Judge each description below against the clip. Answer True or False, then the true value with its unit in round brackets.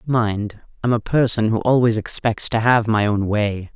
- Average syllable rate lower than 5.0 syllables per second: True (4.4 syllables/s)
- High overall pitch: False (110 Hz)